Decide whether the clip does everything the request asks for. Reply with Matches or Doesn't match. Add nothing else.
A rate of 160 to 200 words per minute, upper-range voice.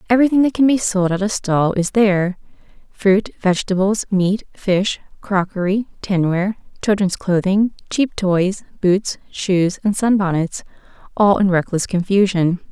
Doesn't match